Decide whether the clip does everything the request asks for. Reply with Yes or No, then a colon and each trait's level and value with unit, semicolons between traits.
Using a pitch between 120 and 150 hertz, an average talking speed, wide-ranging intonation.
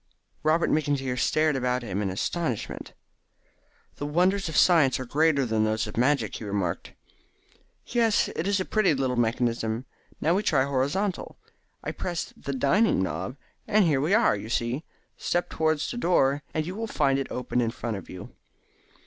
Yes: medium, 140 Hz; average, 175 wpm; wide, 6.0 semitones